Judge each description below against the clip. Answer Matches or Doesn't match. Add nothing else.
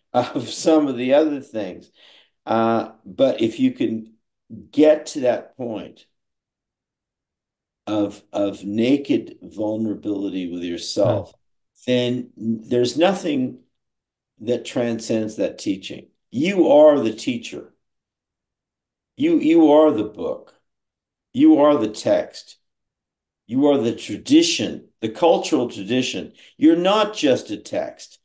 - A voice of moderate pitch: Doesn't match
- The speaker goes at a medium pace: Doesn't match